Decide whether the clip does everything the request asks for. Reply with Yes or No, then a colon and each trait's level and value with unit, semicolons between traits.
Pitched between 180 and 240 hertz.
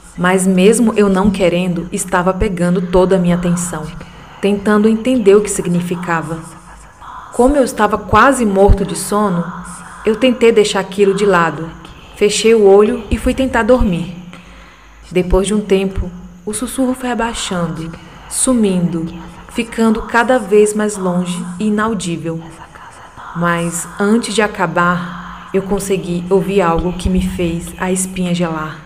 Yes: high, 190 Hz